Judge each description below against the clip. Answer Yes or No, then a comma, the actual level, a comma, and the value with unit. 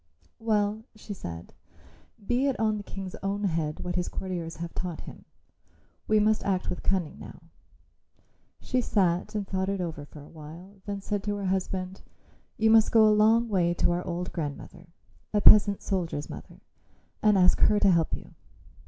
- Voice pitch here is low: No, high, 190 Hz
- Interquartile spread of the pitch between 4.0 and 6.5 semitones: No, average, 3.4 semitones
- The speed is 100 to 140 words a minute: No, average, 180 wpm